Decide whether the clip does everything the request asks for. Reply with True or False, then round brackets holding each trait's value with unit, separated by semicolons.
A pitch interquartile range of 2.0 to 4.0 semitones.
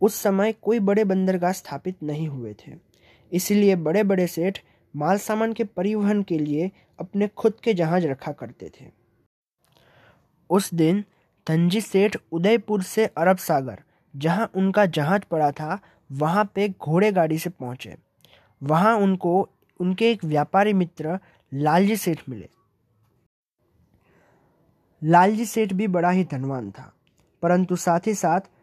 False (4.8 semitones)